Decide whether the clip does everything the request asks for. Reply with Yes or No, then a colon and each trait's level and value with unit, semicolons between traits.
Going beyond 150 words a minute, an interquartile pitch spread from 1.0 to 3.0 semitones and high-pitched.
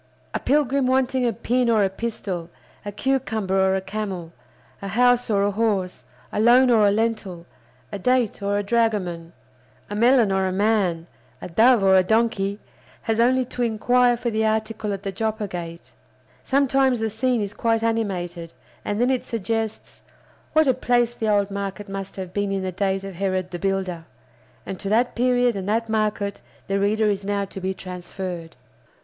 No: average, 185 wpm; average, 3.5 semitones; high, 210 Hz